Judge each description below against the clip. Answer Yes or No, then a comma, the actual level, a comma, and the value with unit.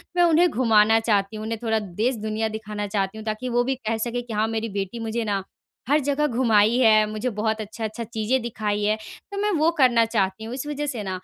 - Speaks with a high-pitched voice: Yes, high, 225 Hz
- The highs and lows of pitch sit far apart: No, narrow, 2.4 semitones